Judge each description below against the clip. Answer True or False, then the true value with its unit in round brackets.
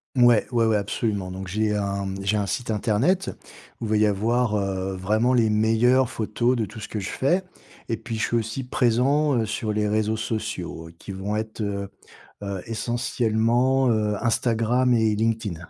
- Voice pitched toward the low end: True (110 Hz)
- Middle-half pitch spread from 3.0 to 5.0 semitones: False (2.5 semitones)